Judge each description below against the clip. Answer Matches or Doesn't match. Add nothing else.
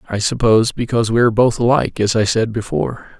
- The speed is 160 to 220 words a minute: Matches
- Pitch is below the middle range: Matches